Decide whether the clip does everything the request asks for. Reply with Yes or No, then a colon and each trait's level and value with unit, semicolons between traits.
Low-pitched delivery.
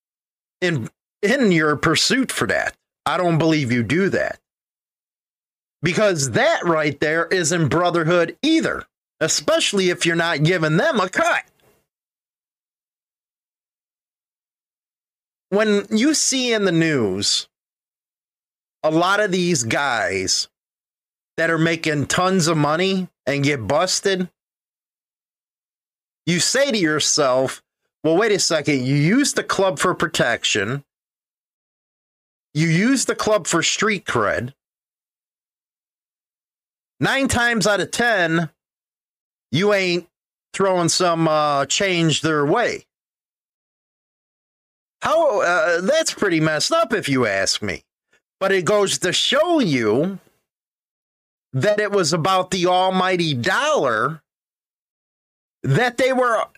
No: medium, 175 Hz